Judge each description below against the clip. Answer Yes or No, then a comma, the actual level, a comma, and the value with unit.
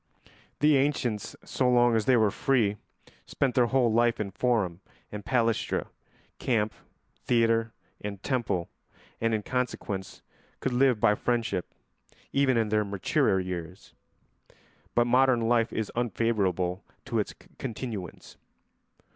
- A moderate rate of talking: No, slow, 125 wpm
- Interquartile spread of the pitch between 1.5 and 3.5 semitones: Yes, average, 3.1 semitones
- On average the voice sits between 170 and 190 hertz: No, low, 115 Hz